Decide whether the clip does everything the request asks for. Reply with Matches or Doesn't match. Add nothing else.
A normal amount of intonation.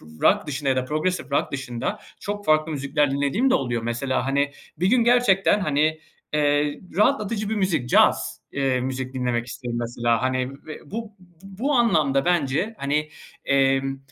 Doesn't match